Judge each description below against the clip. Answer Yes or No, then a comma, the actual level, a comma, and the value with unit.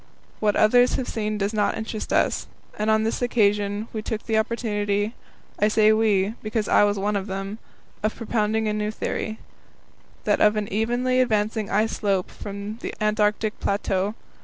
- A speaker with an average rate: Yes, average, 170 wpm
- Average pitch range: No, narrow, 1.2 semitones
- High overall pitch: Yes, high, 215 Hz